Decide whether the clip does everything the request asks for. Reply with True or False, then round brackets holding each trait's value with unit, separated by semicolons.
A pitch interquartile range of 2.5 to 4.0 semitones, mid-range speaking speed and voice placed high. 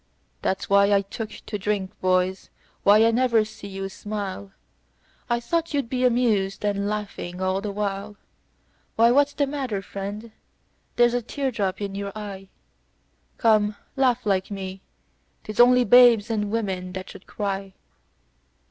True (3.2 semitones; 150 wpm; 210 Hz)